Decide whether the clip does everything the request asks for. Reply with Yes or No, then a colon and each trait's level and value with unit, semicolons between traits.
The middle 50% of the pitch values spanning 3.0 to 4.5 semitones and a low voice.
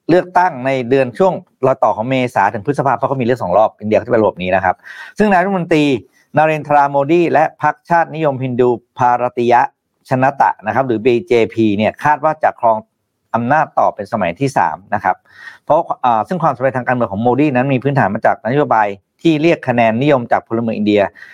Yes: average, 4.1 semitones; low, 130 Hz